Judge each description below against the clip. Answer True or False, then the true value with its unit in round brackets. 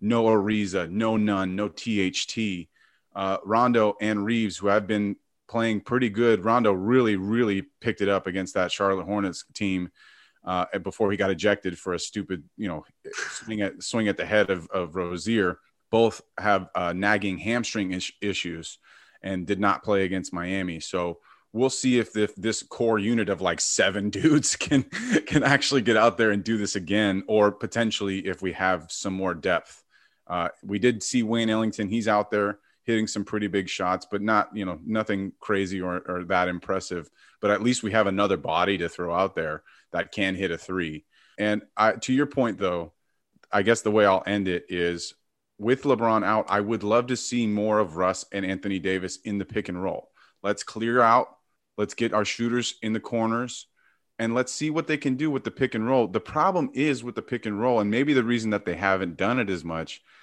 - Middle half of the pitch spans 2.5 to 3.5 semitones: True (3.2 semitones)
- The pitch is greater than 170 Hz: False (105 Hz)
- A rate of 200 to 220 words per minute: True (205 wpm)